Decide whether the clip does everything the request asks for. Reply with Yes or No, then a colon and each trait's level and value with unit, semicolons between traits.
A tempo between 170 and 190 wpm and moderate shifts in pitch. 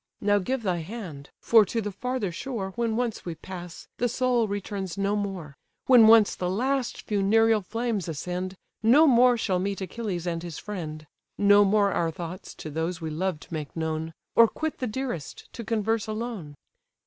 Yes: average, 175 wpm; average, 4.6 semitones